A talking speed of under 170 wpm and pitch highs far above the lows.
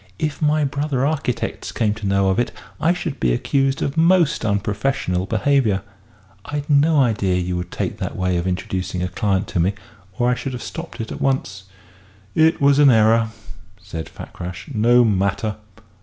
No: average, 175 wpm; wide, 6.7 semitones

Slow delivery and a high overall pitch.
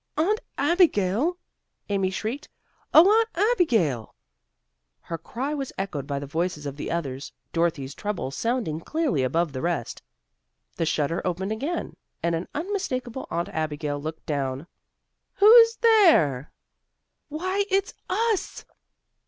Yes: slow, 125 wpm; high, 195 Hz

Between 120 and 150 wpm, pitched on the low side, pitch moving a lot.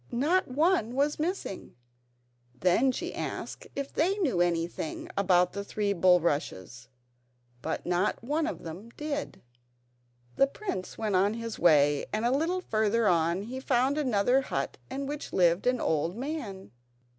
No: average, 145 wpm; high, 220 Hz; wide, 7.9 semitones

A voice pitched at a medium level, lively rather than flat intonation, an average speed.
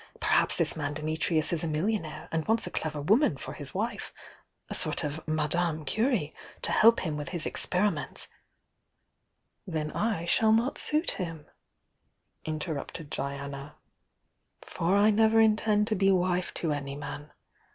Yes: medium, 165 Hz; wide, 5.8 semitones; average, 155 wpm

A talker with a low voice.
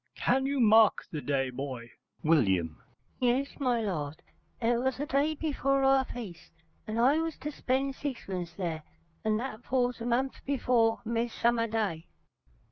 No: high, 235 Hz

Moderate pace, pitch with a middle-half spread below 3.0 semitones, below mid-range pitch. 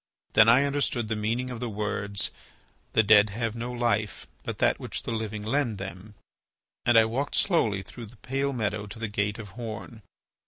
Yes: average, 190 wpm; narrow, 2.6 semitones; low, 110 Hz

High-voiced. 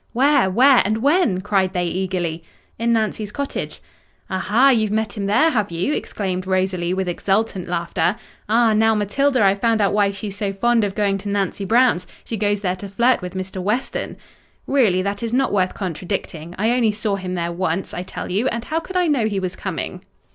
Yes: high, 205 Hz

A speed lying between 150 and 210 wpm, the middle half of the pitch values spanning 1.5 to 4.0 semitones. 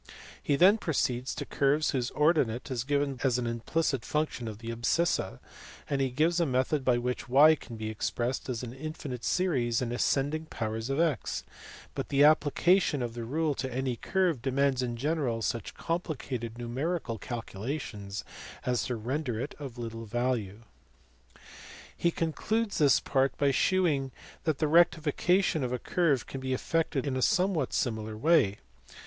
No: average, 165 wpm; average, 4.6 semitones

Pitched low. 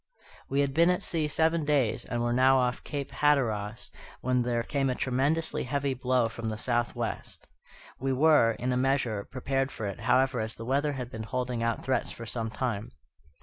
Yes: low, 130 Hz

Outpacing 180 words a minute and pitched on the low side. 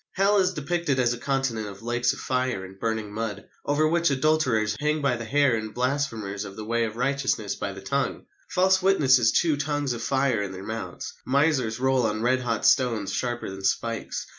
Yes: average, 200 wpm; low, 125 Hz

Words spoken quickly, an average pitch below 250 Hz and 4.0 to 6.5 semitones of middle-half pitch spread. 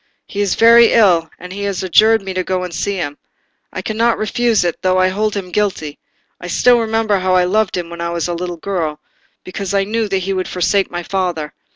No: fast, 230 wpm; high, 190 Hz; average, 3.0 semitones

